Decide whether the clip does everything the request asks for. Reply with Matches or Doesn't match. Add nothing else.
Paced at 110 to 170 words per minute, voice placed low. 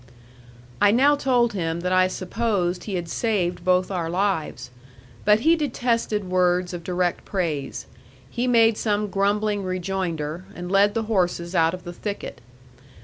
Doesn't match